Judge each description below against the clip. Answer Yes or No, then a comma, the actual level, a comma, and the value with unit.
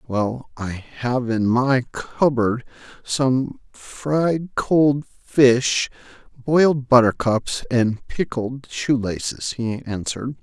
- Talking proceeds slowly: Yes, slow, 90 wpm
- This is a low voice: Yes, low, 125 Hz